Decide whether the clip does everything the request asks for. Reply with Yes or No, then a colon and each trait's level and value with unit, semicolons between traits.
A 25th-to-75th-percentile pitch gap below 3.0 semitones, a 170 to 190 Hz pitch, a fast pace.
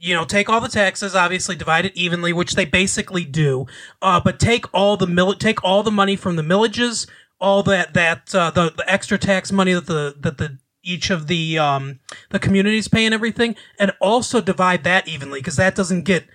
Yes: narrow, 2.6 semitones; medium, 185 Hz; fast, 215 wpm